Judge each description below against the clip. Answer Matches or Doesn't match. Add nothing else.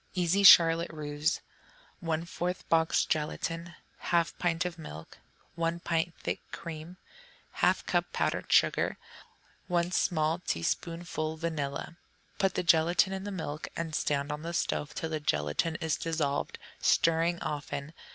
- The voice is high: Doesn't match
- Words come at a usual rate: Doesn't match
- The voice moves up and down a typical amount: Doesn't match